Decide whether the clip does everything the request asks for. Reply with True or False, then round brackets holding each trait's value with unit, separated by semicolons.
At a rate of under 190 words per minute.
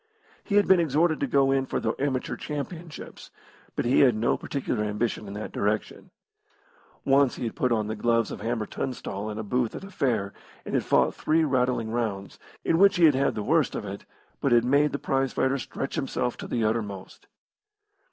False (200 wpm)